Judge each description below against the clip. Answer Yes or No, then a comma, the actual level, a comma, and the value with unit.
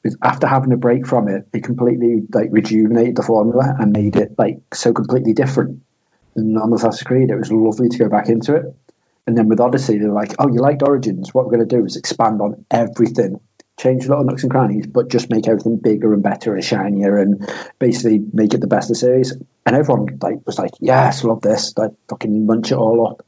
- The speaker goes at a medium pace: No, fast, 230 wpm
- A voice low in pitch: Yes, low, 115 Hz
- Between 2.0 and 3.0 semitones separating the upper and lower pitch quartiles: Yes, narrow, 2.5 semitones